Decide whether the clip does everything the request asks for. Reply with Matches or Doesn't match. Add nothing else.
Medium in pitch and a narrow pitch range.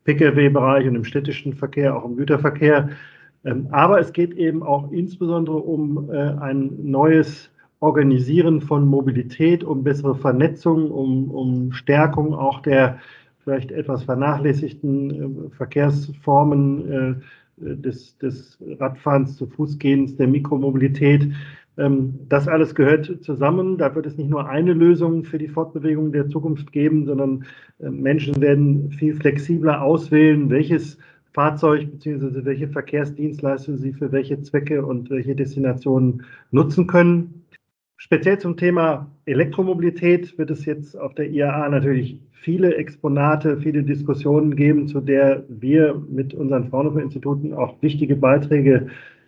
Matches